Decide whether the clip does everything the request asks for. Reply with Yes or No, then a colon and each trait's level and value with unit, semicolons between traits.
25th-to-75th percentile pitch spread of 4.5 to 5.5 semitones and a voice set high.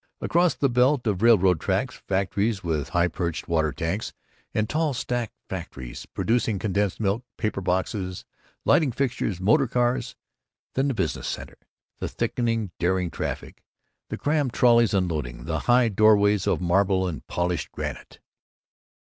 No: average, 5.2 semitones; low, 100 Hz